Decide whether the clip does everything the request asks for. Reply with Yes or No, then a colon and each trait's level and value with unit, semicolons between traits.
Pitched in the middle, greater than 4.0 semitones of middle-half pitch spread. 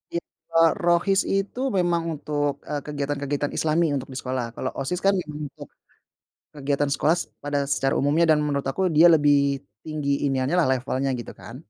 No: medium, 145 Hz; average, 3.0 semitones